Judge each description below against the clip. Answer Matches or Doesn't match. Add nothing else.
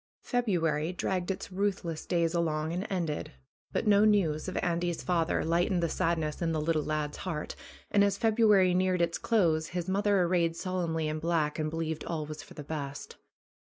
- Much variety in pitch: Doesn't match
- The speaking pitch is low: Doesn't match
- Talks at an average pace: Matches